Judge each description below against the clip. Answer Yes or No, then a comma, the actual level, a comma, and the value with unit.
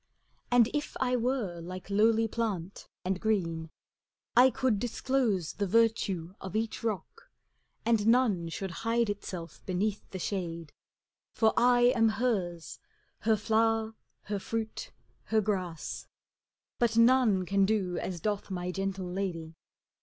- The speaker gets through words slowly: Yes, slow, 130 wpm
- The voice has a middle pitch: No, high, 210 Hz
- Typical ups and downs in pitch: Yes, average, 3.9 semitones